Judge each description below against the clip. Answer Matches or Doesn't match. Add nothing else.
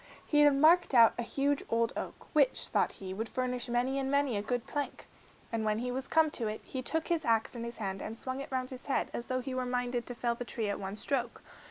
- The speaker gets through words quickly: Matches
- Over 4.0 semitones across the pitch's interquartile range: Doesn't match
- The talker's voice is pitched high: Matches